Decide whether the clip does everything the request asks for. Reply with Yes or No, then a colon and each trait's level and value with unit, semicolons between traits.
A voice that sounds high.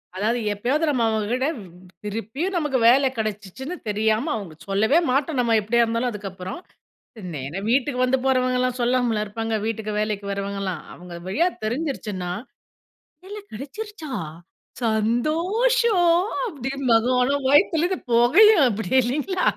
Yes: high, 245 Hz